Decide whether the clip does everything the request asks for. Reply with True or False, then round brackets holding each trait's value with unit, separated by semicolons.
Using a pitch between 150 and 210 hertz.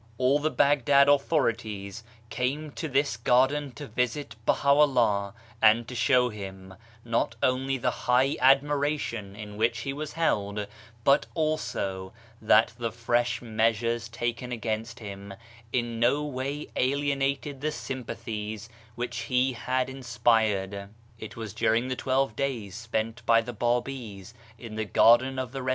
False (120 Hz)